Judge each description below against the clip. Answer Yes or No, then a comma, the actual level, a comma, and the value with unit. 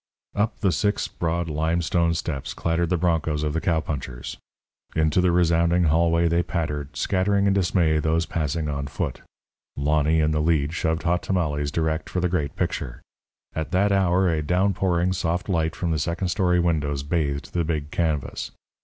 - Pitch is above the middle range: No, very low, 85 Hz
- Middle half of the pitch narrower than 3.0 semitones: Yes, narrow, 2.5 semitones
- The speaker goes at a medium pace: Yes, average, 170 wpm